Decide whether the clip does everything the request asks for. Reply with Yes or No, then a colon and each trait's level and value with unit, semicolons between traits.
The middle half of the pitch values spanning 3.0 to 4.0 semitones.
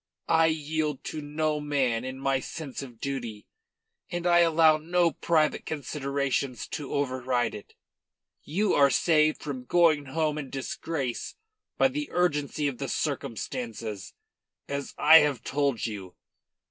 Yes: average, 3.3 semitones